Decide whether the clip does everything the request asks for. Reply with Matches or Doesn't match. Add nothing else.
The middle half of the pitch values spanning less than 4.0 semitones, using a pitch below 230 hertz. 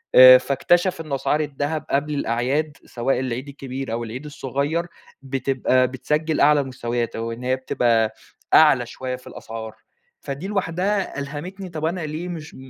Matches